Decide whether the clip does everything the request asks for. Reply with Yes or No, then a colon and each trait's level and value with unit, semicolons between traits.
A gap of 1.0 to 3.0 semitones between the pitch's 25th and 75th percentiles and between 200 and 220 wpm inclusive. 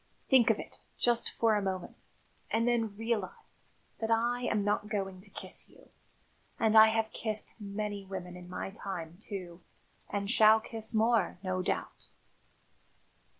No: average, 2.7 semitones; average, 150 wpm